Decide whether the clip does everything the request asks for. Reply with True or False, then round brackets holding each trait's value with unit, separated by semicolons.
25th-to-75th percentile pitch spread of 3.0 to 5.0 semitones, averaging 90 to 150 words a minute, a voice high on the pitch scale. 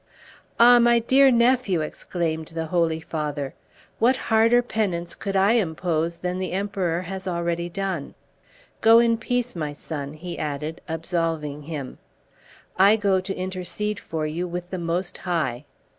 False (4.2 semitones; 145 wpm; 175 Hz)